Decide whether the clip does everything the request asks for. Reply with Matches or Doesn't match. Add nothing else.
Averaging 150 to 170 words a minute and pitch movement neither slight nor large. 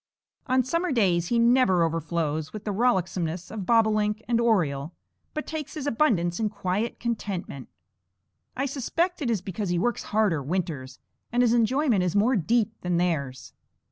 Doesn't match